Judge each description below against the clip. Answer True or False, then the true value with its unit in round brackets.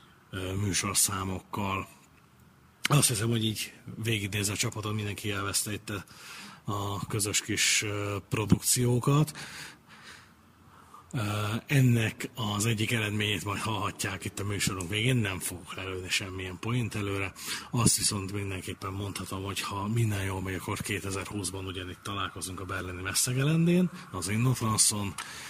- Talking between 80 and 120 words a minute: True (115 wpm)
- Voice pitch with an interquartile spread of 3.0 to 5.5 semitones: False (2.6 semitones)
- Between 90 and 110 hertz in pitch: True (100 Hz)